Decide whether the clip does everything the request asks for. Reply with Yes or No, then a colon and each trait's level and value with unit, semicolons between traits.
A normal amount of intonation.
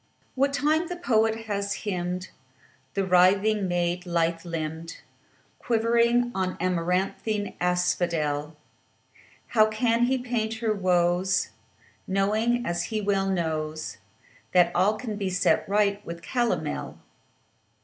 Yes: average, 4.1 semitones